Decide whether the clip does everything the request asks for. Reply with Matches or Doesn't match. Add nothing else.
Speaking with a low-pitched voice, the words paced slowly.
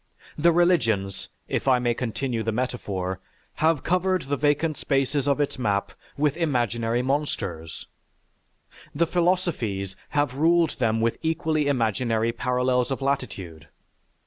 Matches